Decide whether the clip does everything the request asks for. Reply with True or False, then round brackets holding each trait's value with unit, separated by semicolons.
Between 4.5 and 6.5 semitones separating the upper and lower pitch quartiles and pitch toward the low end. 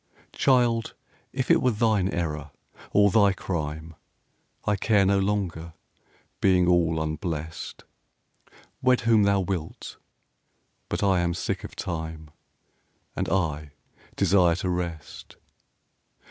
False (3.9 semitones; 90 Hz)